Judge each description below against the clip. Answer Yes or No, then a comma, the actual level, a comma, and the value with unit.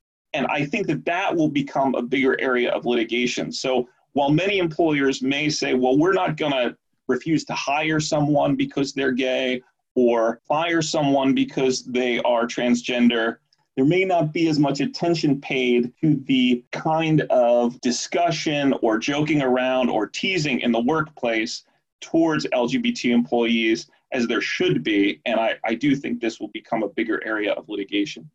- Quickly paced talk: No, average, 165 wpm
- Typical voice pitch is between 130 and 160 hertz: Yes, medium, 140 Hz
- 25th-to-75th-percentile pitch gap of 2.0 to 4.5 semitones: No, average, 4.9 semitones